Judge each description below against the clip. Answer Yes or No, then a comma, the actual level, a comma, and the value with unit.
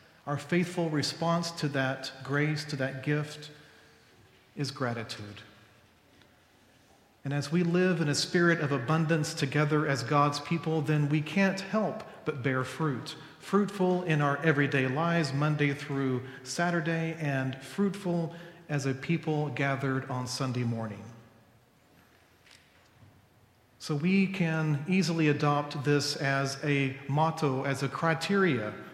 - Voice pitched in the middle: Yes, medium, 145 Hz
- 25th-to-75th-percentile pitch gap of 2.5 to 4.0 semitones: Yes, average, 3.7 semitones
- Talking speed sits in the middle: No, slow, 125 wpm